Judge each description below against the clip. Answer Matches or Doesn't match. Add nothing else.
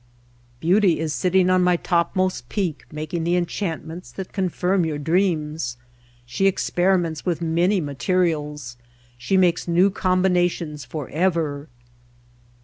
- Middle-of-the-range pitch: Matches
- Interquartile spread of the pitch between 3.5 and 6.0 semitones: Doesn't match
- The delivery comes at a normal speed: Doesn't match